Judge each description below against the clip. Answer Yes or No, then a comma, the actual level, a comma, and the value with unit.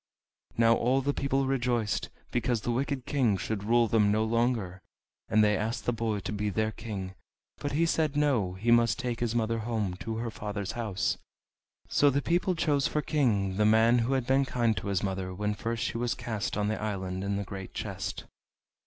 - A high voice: No, low, 115 Hz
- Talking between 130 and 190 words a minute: No, fast, 205 wpm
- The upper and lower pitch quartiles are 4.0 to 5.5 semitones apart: No, average, 3.3 semitones